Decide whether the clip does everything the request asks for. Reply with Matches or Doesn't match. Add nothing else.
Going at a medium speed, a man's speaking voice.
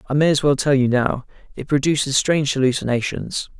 Matches